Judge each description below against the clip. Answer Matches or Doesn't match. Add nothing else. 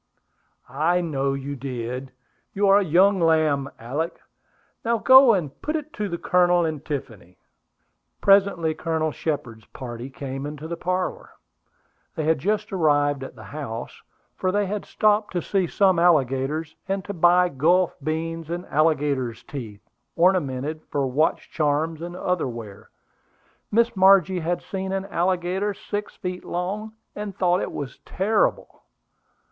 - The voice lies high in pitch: Doesn't match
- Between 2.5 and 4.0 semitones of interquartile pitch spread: Doesn't match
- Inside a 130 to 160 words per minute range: Matches